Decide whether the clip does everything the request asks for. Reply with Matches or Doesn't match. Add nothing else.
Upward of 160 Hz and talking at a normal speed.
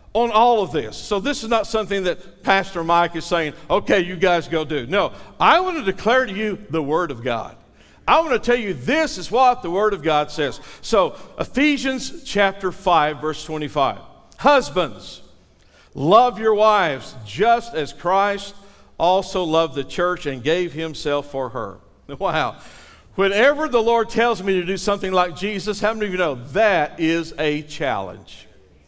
Matches